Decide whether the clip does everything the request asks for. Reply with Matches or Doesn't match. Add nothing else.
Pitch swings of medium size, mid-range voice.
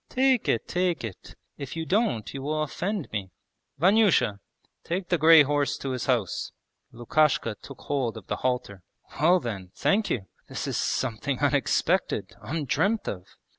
Doesn't match